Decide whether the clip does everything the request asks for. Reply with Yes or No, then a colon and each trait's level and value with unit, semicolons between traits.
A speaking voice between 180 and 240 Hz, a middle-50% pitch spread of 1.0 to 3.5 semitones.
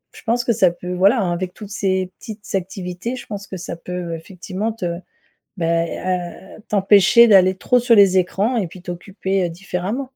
Yes: high, 190 Hz; average, 2.9 semitones